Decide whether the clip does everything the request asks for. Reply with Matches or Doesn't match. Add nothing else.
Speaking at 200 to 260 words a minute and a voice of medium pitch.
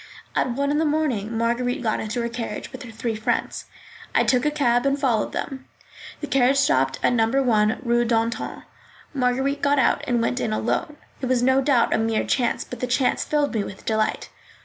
Doesn't match